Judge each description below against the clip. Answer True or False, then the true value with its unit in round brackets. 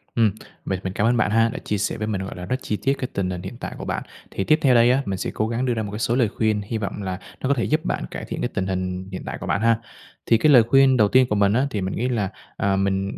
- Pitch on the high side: False (110 Hz)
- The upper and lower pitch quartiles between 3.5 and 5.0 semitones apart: True (3.9 semitones)